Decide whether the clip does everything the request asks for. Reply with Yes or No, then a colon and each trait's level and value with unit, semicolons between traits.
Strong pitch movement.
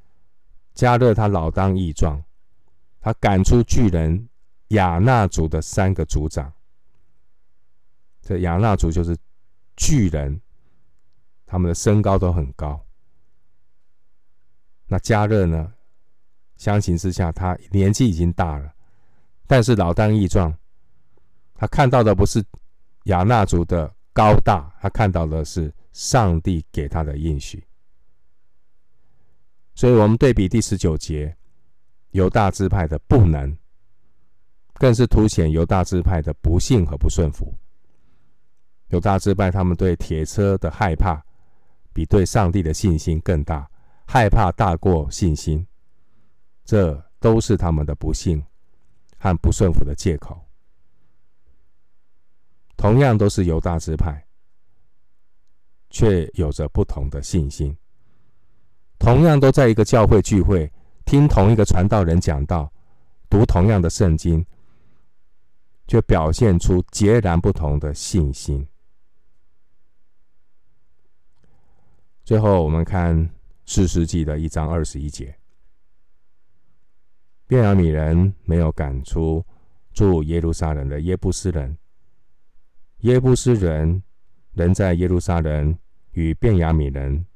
No: average, 4.5 semitones